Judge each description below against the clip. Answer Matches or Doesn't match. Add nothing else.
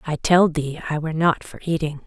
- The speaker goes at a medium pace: Doesn't match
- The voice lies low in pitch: Doesn't match